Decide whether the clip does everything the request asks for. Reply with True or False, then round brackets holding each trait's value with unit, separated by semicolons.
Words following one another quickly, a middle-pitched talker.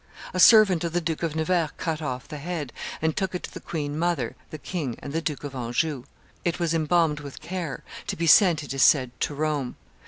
True (225 wpm; 155 Hz)